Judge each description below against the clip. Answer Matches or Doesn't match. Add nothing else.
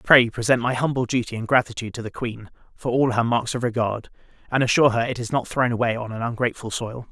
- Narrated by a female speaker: Doesn't match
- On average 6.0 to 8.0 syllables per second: Matches